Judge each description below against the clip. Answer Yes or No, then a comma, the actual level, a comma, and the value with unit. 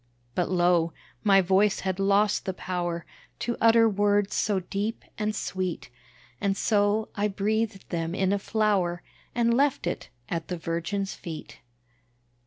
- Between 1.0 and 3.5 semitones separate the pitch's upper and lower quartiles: Yes, average, 2.8 semitones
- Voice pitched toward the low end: No, high, 195 Hz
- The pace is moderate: Yes, average, 145 wpm